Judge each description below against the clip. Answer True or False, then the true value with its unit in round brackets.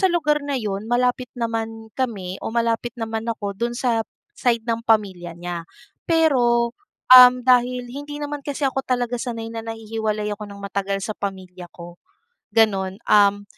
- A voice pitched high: True (225 Hz)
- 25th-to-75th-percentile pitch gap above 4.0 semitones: False (3.5 semitones)